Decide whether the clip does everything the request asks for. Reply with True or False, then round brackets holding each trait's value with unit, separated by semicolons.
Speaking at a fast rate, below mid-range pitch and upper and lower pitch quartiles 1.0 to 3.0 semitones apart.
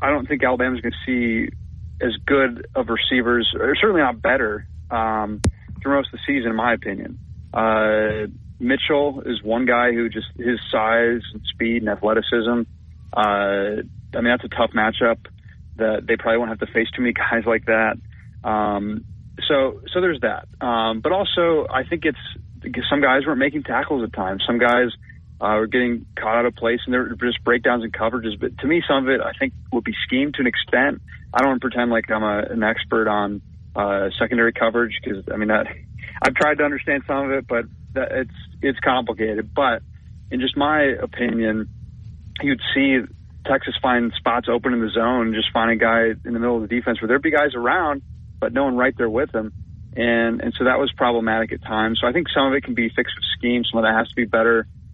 True (215 wpm; 115 Hz; 2.5 semitones)